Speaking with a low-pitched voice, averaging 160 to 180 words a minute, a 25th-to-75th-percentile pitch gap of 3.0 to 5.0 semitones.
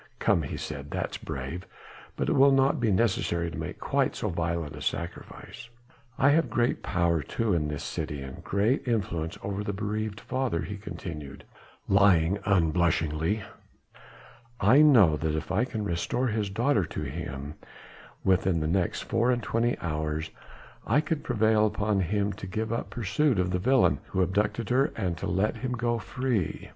No: low, 100 Hz; average, 170 wpm; wide, 5.5 semitones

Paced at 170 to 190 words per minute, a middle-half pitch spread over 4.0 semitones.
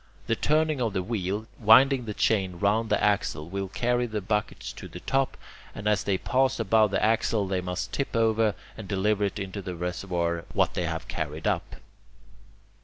No: average, 180 wpm; average, 3.2 semitones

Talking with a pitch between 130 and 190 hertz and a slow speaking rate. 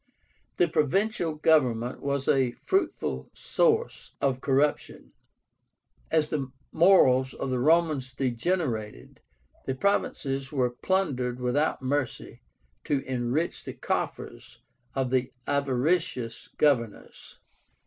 Yes: low, 135 Hz; slow, 100 wpm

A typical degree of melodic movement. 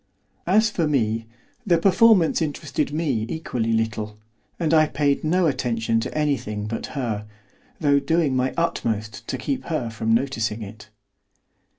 No: wide, 6.3 semitones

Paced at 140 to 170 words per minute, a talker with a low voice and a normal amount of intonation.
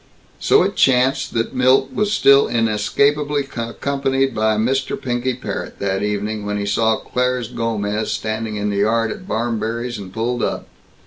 Yes: average, 155 wpm; low, 115 Hz; average, 3.4 semitones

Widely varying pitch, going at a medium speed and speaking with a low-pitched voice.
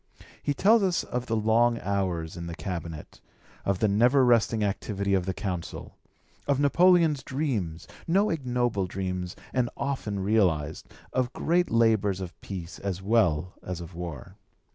Yes: wide, 5.7 semitones; average, 150 wpm; low, 105 Hz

